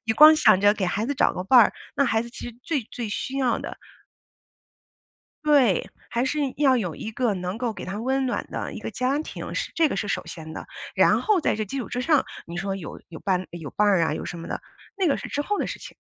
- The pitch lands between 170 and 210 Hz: No, high, 230 Hz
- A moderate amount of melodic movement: No, wide, 5.9 semitones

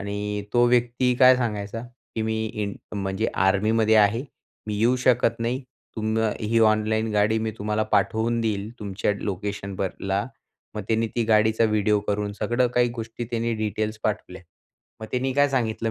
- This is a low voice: Yes, low, 110 Hz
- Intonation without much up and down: Yes, narrow, 2.1 semitones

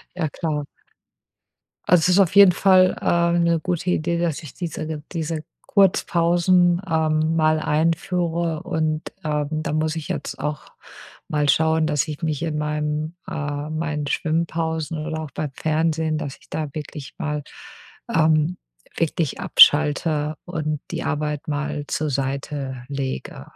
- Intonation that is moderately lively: No, narrow, 1.9 semitones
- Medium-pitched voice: Yes, medium, 155 Hz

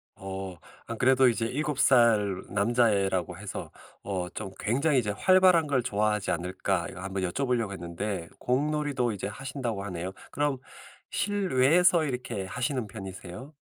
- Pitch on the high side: No, low, 115 Hz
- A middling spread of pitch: No, wide, 5.8 semitones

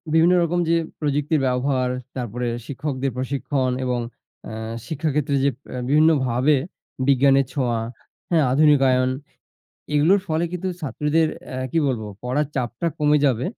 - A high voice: No, medium, 140 Hz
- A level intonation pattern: No, average, 3.0 semitones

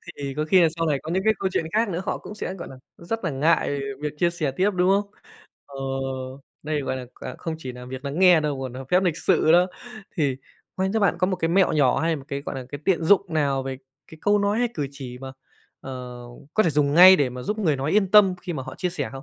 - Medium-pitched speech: Yes, medium, 160 Hz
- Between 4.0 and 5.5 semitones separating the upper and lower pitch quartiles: Yes, average, 5.2 semitones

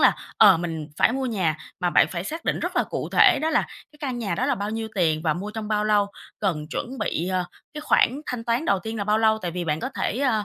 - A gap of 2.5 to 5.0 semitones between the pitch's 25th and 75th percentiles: No, wide, 5.6 semitones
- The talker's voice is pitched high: Yes, high, 215 Hz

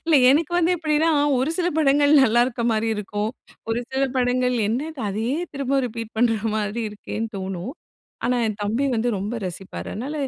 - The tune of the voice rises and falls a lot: No, average, 4.4 semitones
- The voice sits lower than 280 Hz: Yes, high, 240 Hz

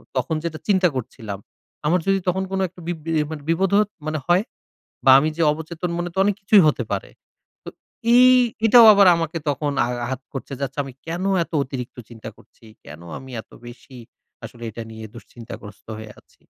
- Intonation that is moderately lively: No, wide, 6.9 semitones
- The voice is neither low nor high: Yes, medium, 155 Hz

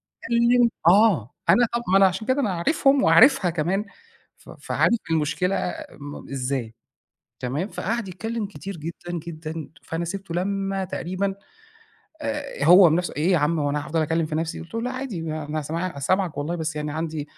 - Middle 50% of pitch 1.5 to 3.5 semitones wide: No, average, 4.3 semitones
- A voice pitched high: No, medium, 175 Hz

